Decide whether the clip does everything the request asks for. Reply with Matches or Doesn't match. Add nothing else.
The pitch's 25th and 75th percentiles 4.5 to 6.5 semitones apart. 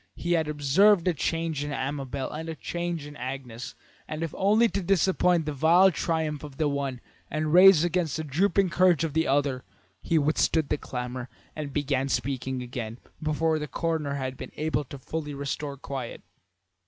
Doesn't match